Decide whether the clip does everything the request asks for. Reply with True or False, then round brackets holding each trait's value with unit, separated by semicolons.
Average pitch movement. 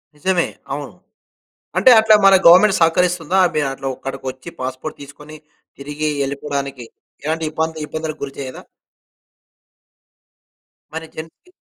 True (3.0 semitones)